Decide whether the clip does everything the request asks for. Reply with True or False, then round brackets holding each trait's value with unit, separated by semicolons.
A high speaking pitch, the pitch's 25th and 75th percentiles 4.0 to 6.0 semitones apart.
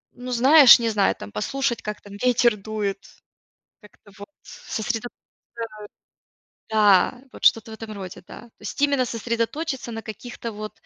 False (225 Hz; 2.7 semitones)